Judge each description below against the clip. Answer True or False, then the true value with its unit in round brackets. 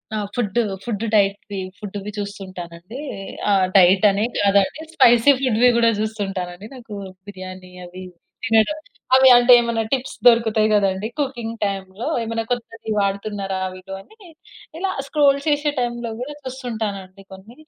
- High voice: True (220 Hz)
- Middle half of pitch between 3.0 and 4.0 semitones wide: True (3.7 semitones)